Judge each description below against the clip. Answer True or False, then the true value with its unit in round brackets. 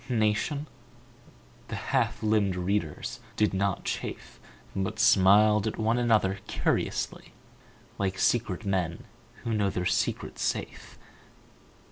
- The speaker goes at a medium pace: False (110 wpm)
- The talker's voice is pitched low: True (105 Hz)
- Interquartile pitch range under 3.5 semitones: True (2.4 semitones)